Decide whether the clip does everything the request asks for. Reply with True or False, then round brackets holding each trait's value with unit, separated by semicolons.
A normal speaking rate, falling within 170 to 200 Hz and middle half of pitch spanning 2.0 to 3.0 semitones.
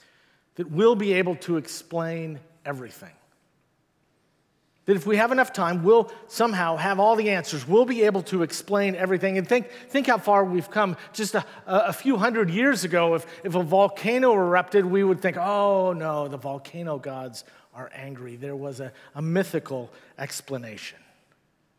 False (165 wpm; 185 Hz; 4.9 semitones)